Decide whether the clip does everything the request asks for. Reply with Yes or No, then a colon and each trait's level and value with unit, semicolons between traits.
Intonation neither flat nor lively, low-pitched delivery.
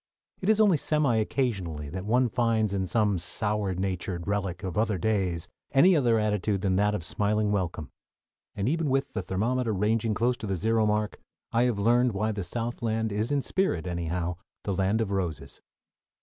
Yes: average, 3.7 semitones; low, 105 Hz